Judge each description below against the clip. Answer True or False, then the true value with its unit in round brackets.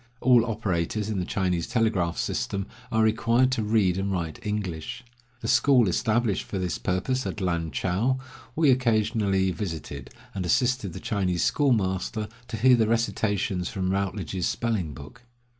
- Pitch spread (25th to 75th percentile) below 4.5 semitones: True (4.0 semitones)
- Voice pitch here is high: False (100 Hz)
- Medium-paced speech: True (150 wpm)